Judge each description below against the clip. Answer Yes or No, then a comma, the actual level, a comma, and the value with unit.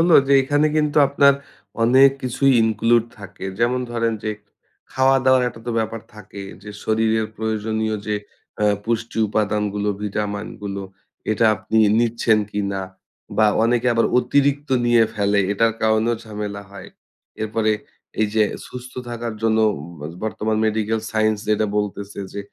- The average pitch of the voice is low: Yes, low, 110 Hz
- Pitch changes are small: Yes, narrow, 2.2 semitones